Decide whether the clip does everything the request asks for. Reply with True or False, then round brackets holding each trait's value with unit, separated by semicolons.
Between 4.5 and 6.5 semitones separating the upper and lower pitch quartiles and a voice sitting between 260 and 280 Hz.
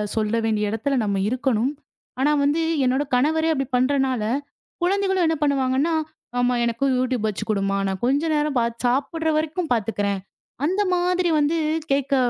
True (5.1 semitones; 265 Hz)